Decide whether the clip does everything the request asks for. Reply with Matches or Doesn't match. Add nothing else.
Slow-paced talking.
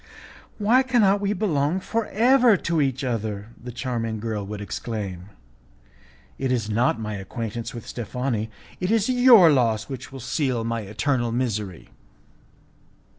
Doesn't match